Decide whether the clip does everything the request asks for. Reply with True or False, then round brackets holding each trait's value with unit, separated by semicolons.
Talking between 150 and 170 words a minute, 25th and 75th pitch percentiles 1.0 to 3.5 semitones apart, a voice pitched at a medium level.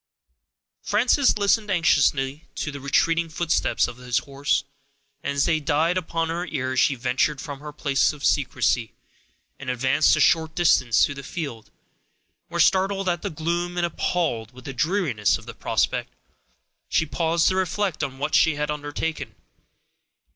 False (160 wpm; 4.0 semitones; 150 Hz)